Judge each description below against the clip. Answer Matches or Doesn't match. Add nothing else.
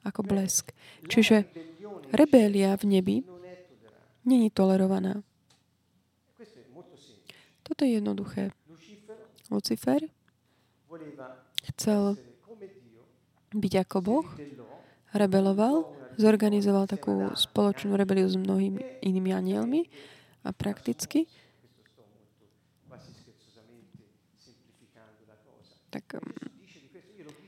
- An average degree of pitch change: Doesn't match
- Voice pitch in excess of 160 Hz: Matches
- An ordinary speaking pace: Doesn't match